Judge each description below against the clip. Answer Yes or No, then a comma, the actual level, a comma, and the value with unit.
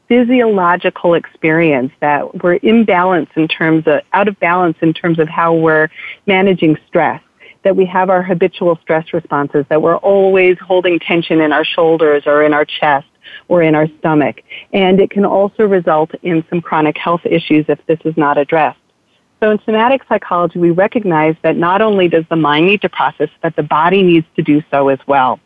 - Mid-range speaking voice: Yes, medium, 170 Hz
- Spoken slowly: No, average, 190 wpm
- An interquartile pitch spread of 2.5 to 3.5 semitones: Yes, average, 3.1 semitones